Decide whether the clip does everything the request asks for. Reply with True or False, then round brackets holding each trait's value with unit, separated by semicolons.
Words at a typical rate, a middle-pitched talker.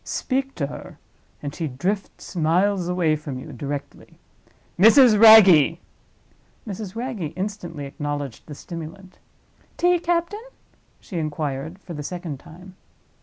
False (120 wpm; 175 Hz)